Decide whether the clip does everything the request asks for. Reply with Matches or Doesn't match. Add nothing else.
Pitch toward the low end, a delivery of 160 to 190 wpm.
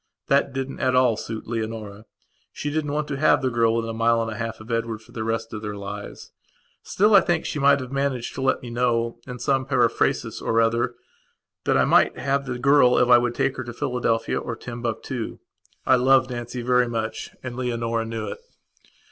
Doesn't match